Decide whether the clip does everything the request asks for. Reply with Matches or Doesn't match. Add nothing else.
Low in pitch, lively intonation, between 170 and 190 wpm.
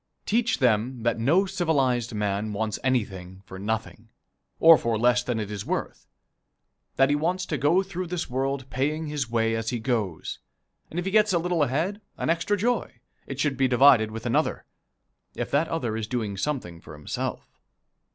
Matches